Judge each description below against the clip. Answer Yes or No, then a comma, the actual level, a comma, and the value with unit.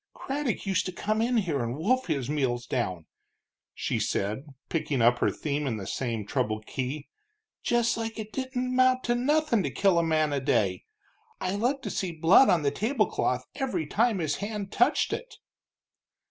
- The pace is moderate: Yes, average, 180 wpm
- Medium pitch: Yes, medium, 175 Hz